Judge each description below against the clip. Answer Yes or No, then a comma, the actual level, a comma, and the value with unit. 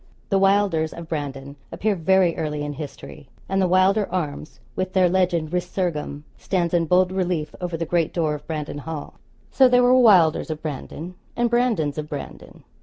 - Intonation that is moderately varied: Yes, average, 3.8 semitones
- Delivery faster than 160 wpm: Yes, average, 180 wpm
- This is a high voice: No, medium, 170 Hz